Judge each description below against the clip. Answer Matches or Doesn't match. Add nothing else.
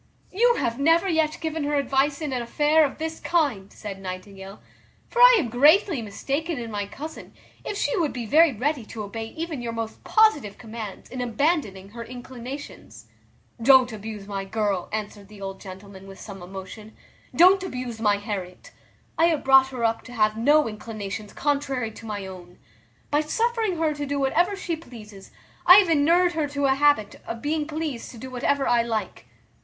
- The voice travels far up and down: Matches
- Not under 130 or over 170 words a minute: Doesn't match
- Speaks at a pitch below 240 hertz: Doesn't match